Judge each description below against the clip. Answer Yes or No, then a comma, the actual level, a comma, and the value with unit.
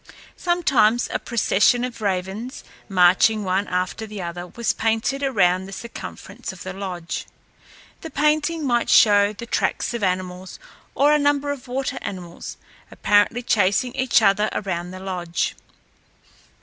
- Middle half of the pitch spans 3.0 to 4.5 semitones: No, average, 4.9 semitones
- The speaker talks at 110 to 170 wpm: Yes, average, 140 wpm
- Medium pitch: No, high, 210 Hz